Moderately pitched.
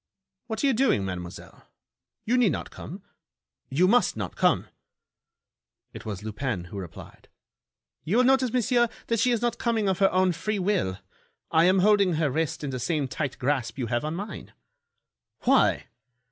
Yes: medium, 180 Hz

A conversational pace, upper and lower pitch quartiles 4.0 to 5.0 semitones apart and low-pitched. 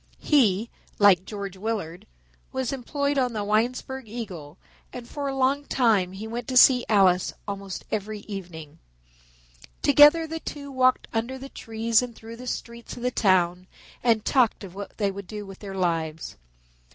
No: average, 165 wpm; average, 4.6 semitones; high, 220 Hz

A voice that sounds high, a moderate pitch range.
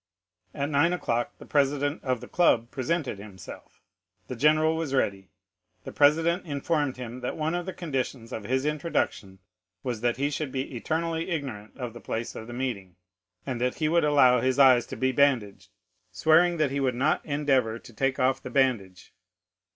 No: low, 135 Hz; average, 4.0 semitones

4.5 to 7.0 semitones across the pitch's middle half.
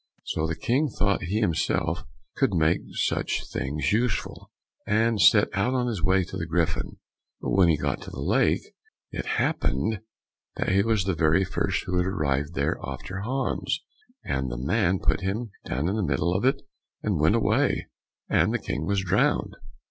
Yes: average, 4.9 semitones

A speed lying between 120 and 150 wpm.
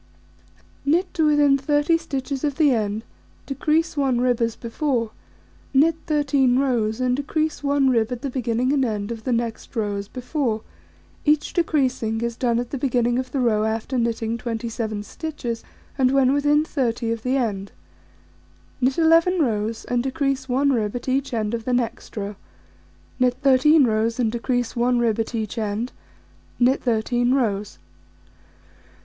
No: average, 165 wpm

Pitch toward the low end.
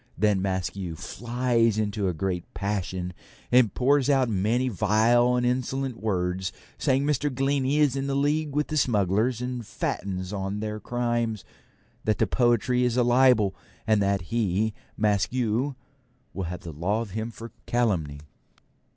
Yes: low, 110 Hz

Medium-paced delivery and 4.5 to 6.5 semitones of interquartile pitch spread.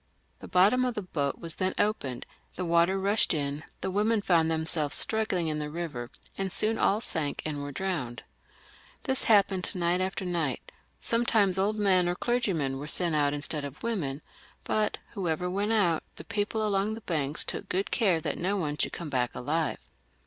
Yes: average, 185 wpm; average, 5.2 semitones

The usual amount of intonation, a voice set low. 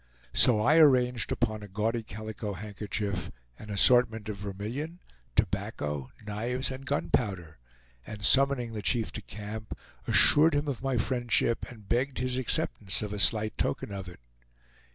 Yes: average, 3.5 semitones; low, 110 Hz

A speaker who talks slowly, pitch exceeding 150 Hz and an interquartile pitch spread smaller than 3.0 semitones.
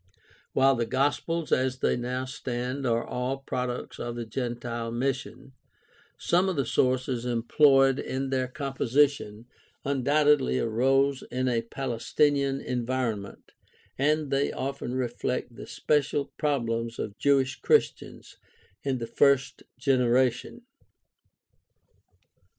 No: slow, 115 wpm; low, 130 Hz; narrow, 2.4 semitones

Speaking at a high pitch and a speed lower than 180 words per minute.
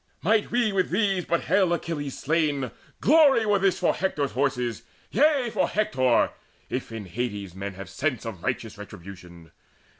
No: medium, 145 Hz; average, 155 wpm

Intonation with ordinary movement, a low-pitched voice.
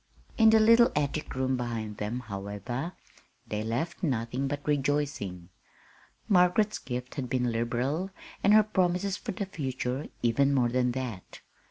No: wide, 6.6 semitones; low, 130 Hz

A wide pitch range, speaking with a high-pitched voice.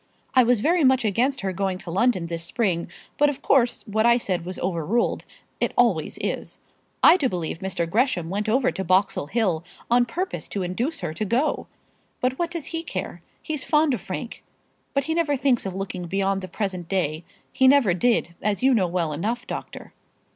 Yes: wide, 6.1 semitones; high, 215 Hz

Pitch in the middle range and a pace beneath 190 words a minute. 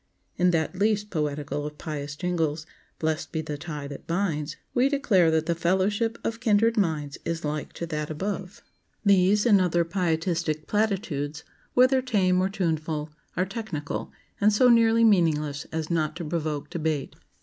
Yes: medium, 170 Hz; average, 160 wpm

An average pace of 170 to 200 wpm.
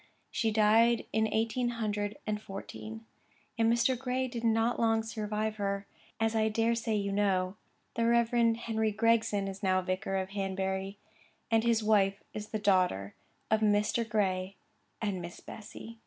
No: average, 155 wpm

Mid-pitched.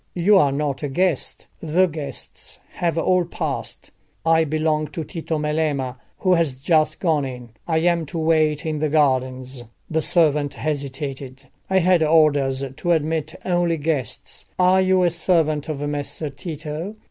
Yes: medium, 155 Hz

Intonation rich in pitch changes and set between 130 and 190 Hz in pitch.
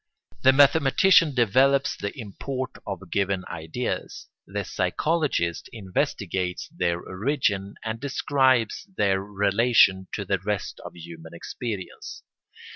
No: wide, 5.8 semitones; low, 105 Hz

